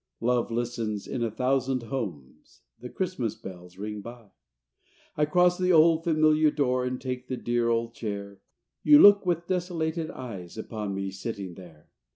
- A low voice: Yes, low, 120 Hz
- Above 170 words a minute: No, average, 160 wpm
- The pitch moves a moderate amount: No, wide, 6.9 semitones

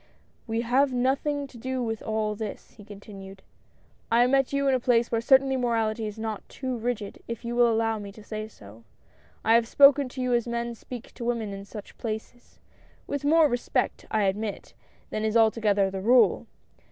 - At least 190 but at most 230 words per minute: Yes, average, 200 wpm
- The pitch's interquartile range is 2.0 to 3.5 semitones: Yes, narrow, 2.6 semitones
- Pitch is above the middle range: Yes, high, 230 Hz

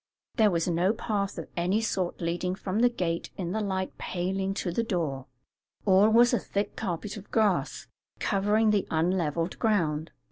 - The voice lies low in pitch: No, high, 190 Hz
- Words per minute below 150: No, average, 170 wpm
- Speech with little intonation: No, average, 3.5 semitones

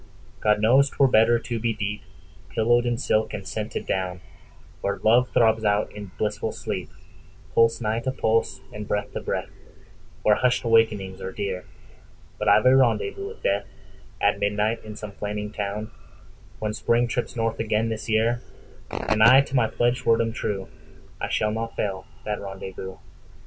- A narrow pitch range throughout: Yes, narrow, 2.2 semitones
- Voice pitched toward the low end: Yes, low, 110 Hz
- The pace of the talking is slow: No, average, 145 wpm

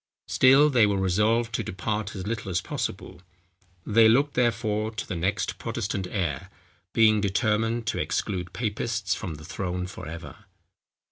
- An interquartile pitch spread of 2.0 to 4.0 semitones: Yes, average, 3.6 semitones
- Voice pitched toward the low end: Yes, low, 105 Hz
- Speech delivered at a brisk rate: No, average, 150 wpm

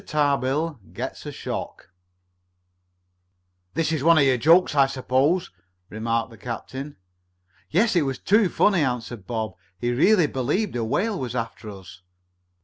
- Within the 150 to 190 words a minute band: No, average, 140 wpm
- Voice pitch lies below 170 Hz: Yes, low, 135 Hz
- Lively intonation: Yes, wide, 5.8 semitones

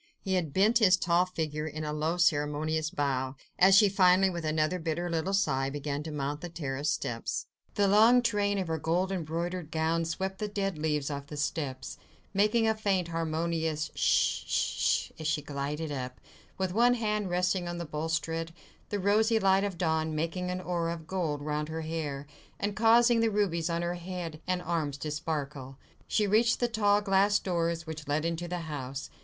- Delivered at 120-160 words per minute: No, average, 185 wpm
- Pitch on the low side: No, medium, 170 Hz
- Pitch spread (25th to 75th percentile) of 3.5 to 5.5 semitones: Yes, average, 3.9 semitones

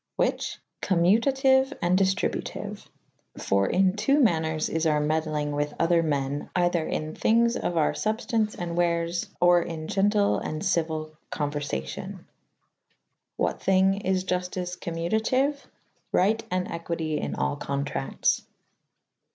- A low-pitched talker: No, medium, 175 Hz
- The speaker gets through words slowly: Yes, slow, 130 wpm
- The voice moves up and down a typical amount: Yes, average, 3.8 semitones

